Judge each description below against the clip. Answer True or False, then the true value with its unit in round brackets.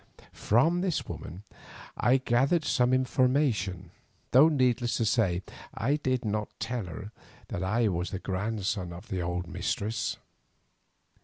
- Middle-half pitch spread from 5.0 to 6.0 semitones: True (5.3 semitones)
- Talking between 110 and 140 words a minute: True (135 wpm)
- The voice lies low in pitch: True (115 Hz)